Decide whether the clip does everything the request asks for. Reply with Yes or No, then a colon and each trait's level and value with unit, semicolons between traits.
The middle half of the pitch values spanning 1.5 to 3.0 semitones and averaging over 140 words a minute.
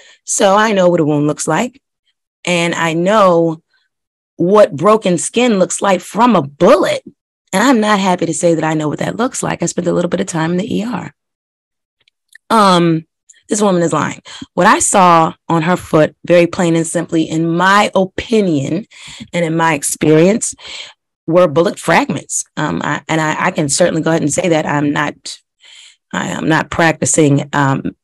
No: average, 3.4 semitones; average, 180 wpm